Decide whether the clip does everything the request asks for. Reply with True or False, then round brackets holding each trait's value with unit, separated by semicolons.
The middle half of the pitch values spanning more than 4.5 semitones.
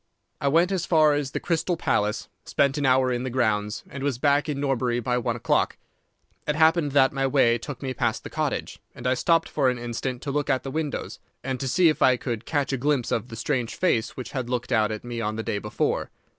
False (3.3 semitones)